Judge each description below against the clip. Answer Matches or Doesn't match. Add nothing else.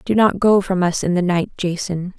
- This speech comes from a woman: Matches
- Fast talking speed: Matches